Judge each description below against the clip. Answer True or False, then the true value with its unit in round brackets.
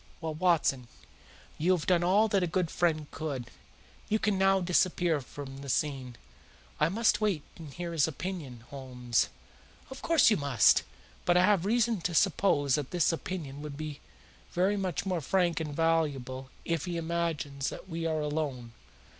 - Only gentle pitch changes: False (4.3 semitones)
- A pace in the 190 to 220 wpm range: False (170 wpm)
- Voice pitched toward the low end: False (165 Hz)